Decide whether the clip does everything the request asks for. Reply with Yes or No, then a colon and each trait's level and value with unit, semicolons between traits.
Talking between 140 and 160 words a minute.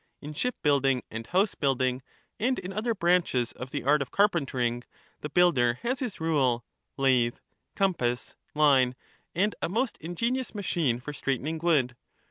Yes: average, 150 wpm